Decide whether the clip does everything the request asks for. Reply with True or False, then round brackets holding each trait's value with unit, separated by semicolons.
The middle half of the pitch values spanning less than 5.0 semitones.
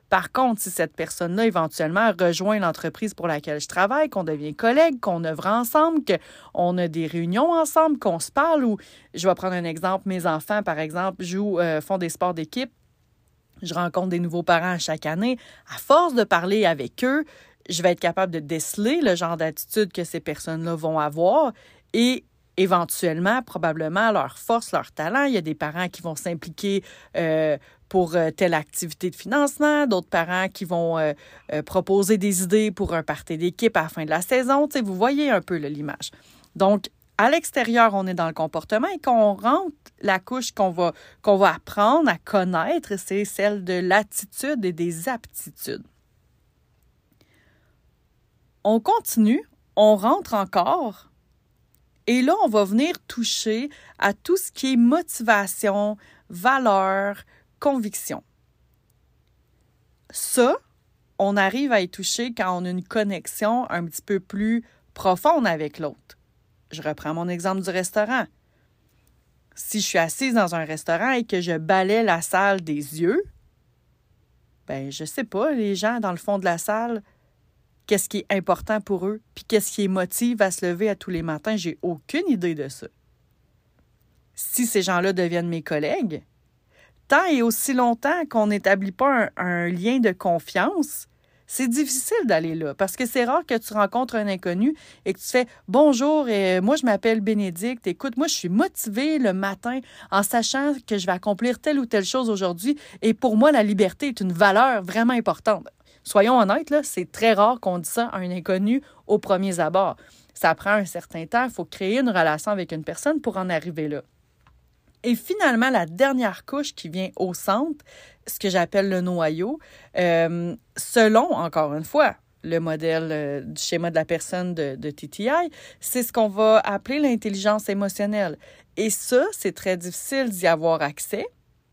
False (5.6 semitones)